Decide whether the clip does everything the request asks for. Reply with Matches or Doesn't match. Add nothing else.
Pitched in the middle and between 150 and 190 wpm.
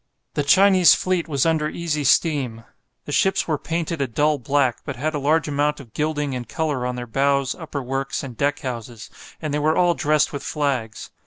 Doesn't match